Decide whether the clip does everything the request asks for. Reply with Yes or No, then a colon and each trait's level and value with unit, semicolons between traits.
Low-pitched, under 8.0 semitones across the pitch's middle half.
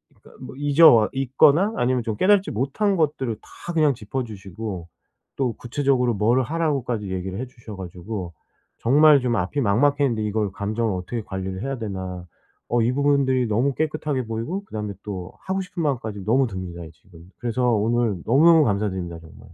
Yes: low, 120 Hz; wide, 5.5 semitones